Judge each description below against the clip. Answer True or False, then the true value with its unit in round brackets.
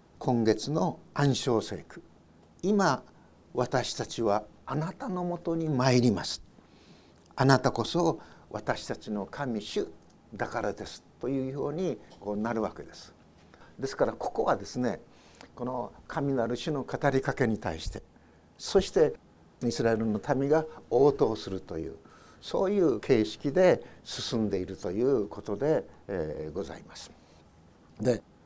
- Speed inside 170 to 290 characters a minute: True (255 characters per minute)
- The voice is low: True (120 Hz)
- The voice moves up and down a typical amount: True (5.0 semitones)